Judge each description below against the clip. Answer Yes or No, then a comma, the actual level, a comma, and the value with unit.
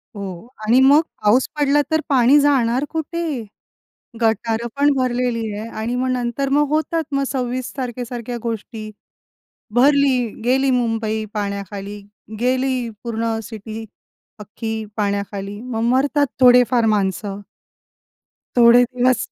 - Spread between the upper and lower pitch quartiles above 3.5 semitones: No, average, 3.0 semitones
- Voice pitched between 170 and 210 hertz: No, high, 240 Hz